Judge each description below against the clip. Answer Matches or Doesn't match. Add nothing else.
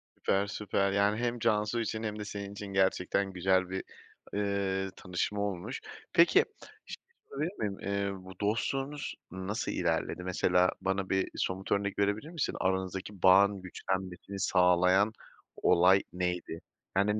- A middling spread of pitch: Doesn't match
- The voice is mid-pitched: Doesn't match